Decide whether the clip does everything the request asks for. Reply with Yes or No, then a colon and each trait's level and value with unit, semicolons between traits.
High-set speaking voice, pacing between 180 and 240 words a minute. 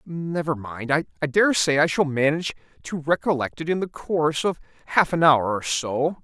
No: medium, 155 Hz; average, 190 wpm